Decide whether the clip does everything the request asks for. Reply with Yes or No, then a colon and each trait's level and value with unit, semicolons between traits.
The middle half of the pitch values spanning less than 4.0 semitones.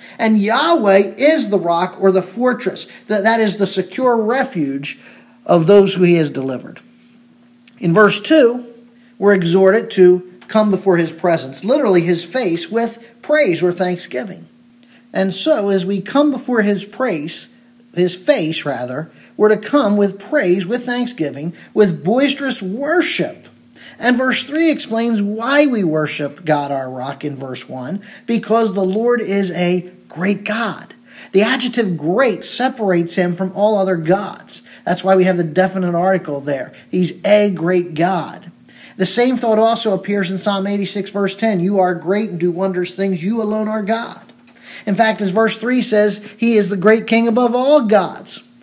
No: average, 4.4 semitones